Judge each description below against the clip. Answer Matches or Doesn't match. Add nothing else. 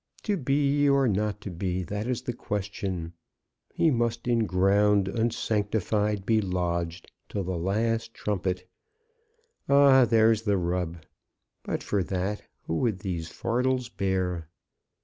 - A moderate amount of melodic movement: Matches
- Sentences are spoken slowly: Matches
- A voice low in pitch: Matches